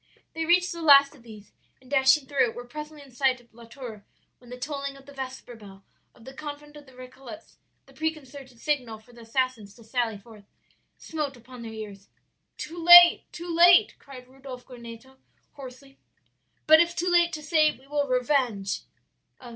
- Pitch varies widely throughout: No, average, 3.8 semitones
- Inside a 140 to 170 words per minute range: No, average, 185 wpm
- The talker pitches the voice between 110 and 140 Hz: No, very high, 265 Hz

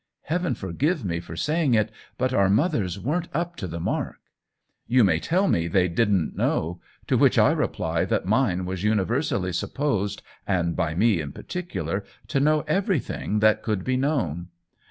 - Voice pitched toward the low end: Yes, low, 105 Hz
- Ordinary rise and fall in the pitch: No, wide, 8.4 semitones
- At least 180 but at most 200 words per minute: No, average, 170 wpm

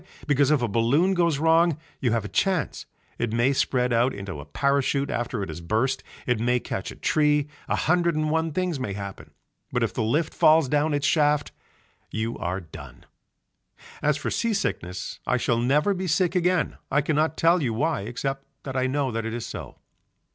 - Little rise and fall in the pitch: No, average, 5.2 semitones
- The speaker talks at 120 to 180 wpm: No, average, 200 wpm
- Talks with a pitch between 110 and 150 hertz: Yes, medium, 140 Hz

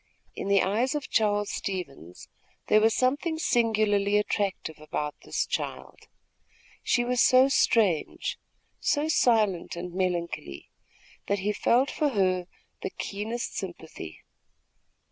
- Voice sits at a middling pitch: No, high, 205 Hz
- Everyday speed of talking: No, slow, 120 wpm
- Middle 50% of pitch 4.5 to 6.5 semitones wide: Yes, average, 4.9 semitones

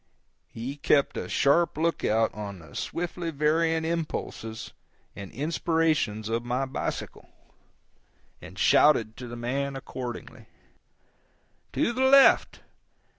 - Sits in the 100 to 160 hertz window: Yes, medium, 140 Hz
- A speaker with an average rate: No, slow, 110 wpm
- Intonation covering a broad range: Yes, wide, 6.0 semitones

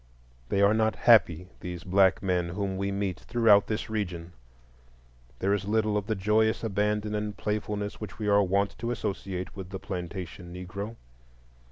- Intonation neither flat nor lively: No, narrow, 2.3 semitones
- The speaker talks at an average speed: Yes, average, 165 wpm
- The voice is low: Yes, low, 100 Hz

